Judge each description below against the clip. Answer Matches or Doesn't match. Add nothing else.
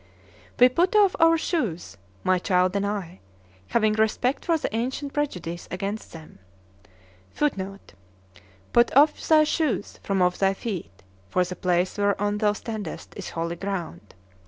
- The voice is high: Matches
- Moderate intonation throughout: Doesn't match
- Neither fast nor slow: Matches